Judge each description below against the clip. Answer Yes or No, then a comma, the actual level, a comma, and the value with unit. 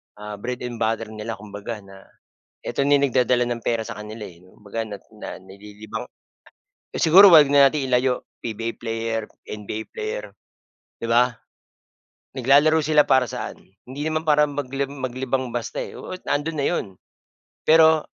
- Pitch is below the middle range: Yes, low, 125 Hz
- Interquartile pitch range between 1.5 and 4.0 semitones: No, average, 4.6 semitones